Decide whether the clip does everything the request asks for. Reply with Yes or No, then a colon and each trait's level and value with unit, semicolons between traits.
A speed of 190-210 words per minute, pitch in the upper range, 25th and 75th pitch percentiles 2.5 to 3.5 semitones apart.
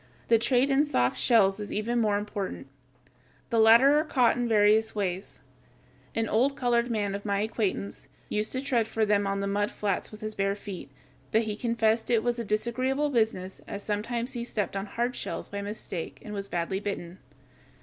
Yes: average, 195 wpm; high, 215 Hz; average, 2.8 semitones